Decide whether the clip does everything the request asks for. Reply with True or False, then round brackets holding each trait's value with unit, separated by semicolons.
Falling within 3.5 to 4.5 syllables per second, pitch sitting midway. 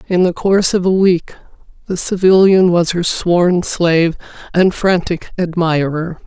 True (4.3 syllables/s; 175 Hz)